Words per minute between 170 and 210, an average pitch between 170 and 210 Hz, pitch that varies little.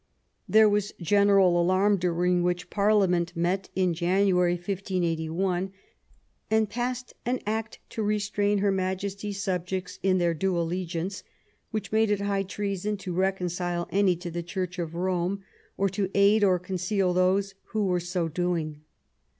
No: average, 150 wpm; medium, 185 Hz; narrow, 2.3 semitones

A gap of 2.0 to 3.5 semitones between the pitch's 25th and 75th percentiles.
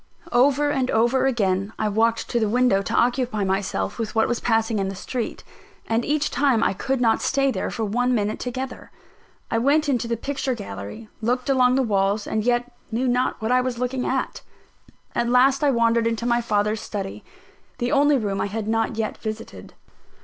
Yes: average, 2.8 semitones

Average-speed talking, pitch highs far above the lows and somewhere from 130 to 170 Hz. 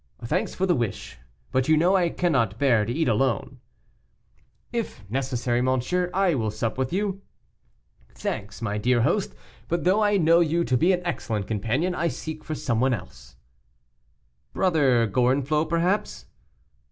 Yes: average, 155 wpm; wide, 6.9 semitones; medium, 140 Hz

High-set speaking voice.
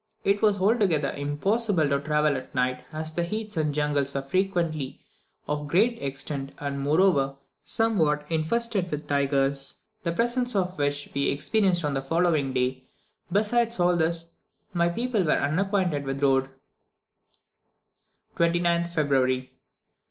No: medium, 155 Hz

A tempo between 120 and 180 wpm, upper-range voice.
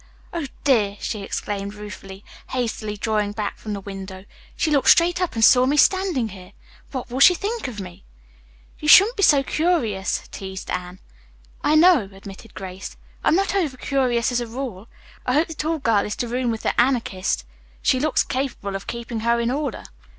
No: average, 190 wpm; high, 235 Hz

